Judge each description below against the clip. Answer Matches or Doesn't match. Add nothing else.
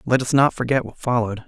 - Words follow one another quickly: Matches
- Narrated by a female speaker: Doesn't match